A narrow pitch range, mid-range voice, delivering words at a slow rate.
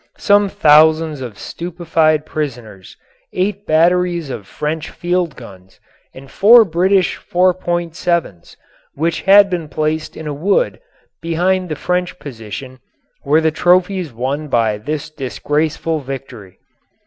No: average, 4.6 semitones; medium, 160 Hz; slow, 120 wpm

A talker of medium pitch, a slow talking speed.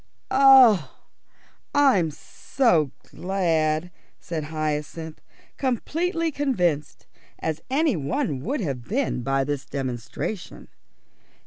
Yes: medium, 170 Hz; slow, 90 wpm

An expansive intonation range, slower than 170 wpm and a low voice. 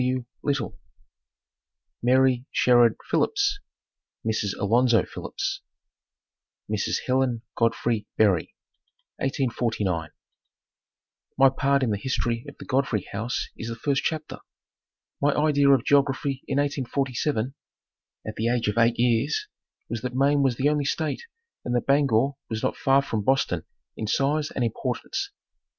No: average, 3.3 semitones; slow, 135 wpm; low, 130 Hz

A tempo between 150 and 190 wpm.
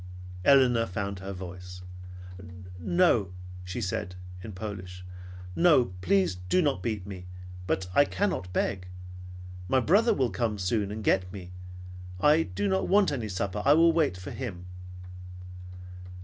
No: average, 140 wpm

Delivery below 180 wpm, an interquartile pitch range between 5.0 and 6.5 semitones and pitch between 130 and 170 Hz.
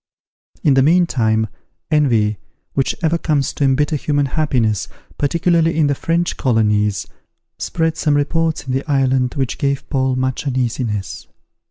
No: average, 140 wpm; average, 3.6 semitones; low, 135 Hz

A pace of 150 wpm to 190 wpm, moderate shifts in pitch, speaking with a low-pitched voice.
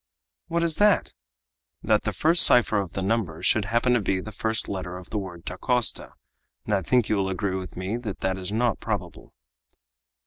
No: average, 200 wpm; average, 4.2 semitones; low, 105 Hz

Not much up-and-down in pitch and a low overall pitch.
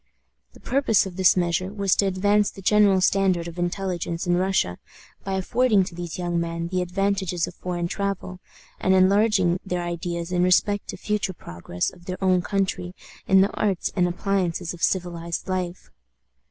No: narrow, 2.1 semitones; medium, 185 Hz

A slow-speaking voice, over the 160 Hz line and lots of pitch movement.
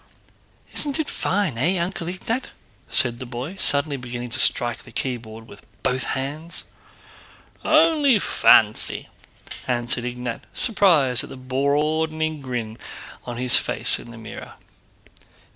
No: slow, 125 wpm; low, 135 Hz; wide, 5.9 semitones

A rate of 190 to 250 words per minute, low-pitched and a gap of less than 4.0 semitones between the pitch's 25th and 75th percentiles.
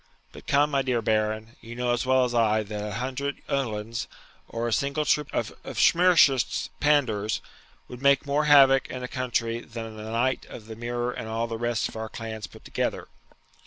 Yes: average, 195 wpm; low, 120 Hz; average, 3.3 semitones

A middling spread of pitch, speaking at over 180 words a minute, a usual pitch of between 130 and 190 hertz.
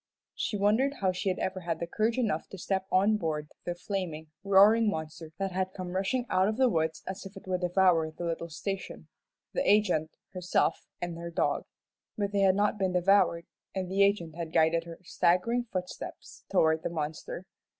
Yes: average, 3.0 semitones; average, 190 wpm; medium, 185 Hz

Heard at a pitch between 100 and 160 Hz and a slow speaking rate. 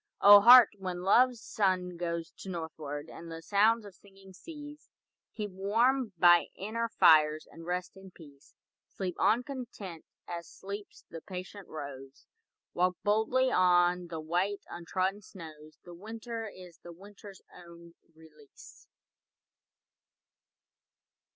No: medium, 185 Hz; slow, 125 wpm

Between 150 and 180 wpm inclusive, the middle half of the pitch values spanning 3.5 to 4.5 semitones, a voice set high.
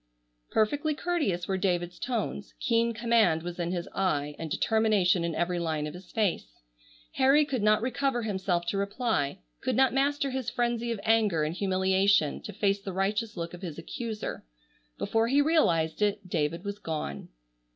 No: average, 170 wpm; average, 5.3 semitones; high, 200 Hz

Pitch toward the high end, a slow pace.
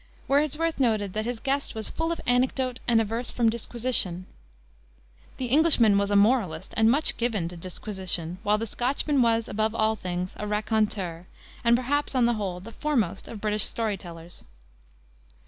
No: high, 220 Hz; average, 165 wpm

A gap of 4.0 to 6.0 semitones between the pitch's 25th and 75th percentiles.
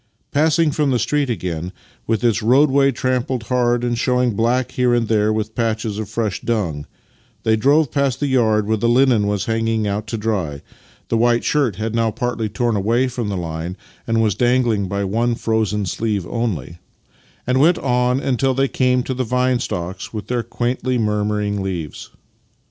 No: average, 3.2 semitones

